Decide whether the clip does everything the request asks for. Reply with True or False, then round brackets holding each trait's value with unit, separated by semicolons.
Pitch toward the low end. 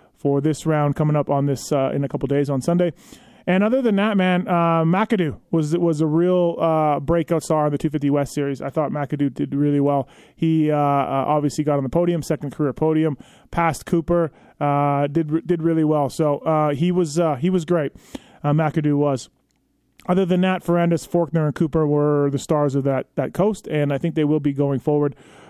False (155 Hz)